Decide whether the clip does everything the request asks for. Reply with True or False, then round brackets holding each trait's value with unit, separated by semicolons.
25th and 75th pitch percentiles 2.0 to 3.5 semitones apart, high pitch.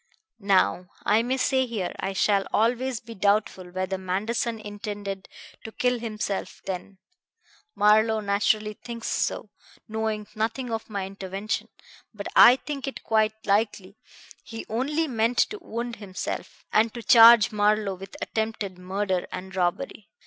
True (2.7 semitones; 215 Hz)